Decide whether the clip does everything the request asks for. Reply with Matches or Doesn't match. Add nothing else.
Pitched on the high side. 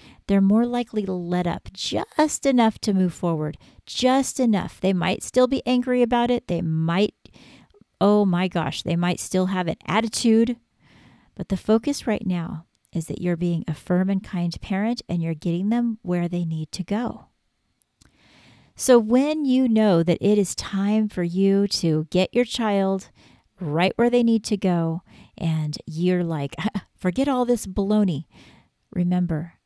Matches